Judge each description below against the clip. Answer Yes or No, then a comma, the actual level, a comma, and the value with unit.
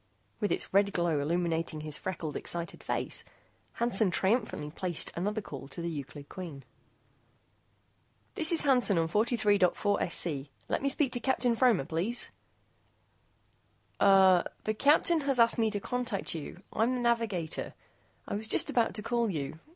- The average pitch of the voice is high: Yes, high, 200 Hz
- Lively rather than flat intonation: Yes, wide, 5.9 semitones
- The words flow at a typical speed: Yes, average, 150 wpm